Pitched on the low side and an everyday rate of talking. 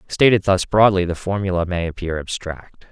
Yes: very low, 95 Hz; average, 165 wpm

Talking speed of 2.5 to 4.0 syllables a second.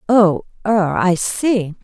Yes: 2.8 syllables/s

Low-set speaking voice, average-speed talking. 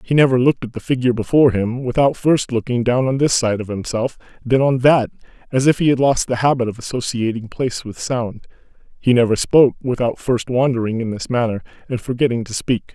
No: low, 125 Hz; fast, 210 wpm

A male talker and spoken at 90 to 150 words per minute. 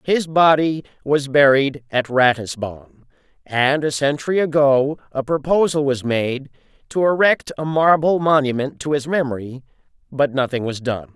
Yes: male; average, 140 wpm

